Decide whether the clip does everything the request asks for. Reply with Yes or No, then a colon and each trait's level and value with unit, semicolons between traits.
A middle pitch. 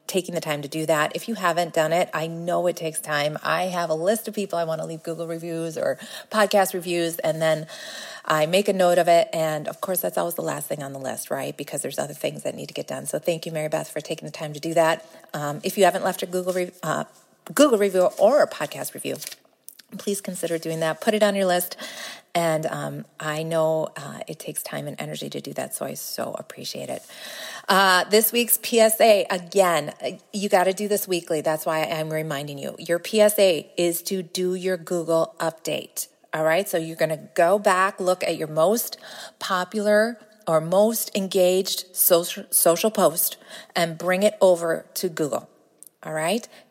Yes: medium, 175 Hz